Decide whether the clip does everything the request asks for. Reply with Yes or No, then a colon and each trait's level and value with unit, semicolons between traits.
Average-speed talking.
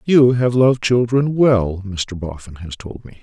Yes: average, 185 wpm